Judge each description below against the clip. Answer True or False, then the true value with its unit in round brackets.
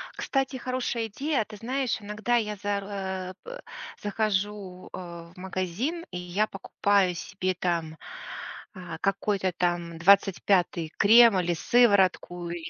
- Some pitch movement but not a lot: True (3.4 semitones)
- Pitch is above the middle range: True (195 Hz)